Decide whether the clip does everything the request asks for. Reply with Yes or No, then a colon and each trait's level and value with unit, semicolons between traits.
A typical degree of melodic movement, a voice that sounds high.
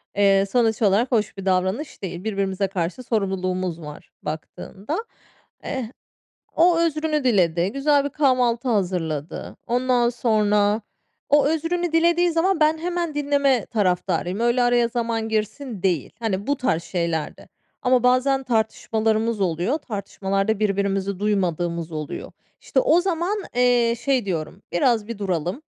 No: wide, 5.9 semitones; high, 220 Hz